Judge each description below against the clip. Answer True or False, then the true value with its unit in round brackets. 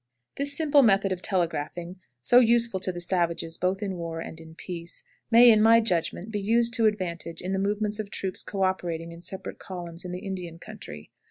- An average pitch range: True (4.0 semitones)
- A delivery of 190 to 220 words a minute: True (200 wpm)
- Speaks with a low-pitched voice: False (190 Hz)